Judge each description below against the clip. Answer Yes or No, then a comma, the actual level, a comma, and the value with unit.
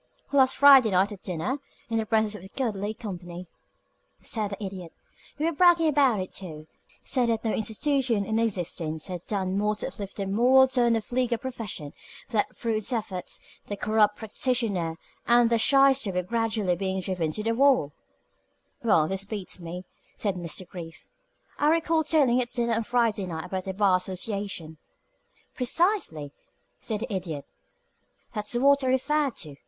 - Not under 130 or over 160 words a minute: No, average, 175 wpm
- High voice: Yes, high, 215 Hz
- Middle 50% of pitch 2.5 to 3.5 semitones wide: No, average, 4.9 semitones